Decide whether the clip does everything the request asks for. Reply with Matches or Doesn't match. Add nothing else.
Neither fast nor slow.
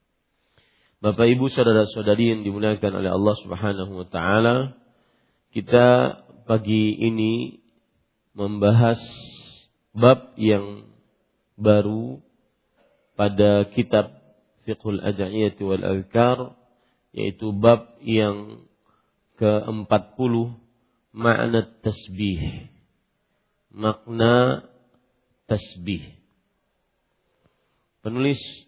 Doesn't match